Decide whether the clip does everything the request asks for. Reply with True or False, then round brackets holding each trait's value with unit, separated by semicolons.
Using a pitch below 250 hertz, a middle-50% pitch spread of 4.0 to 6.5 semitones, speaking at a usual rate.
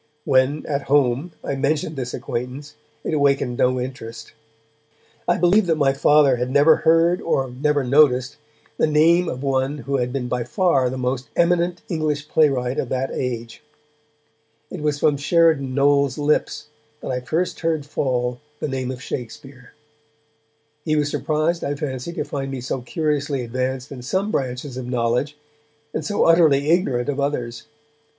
False (140 Hz; 3.1 semitones; 160 wpm)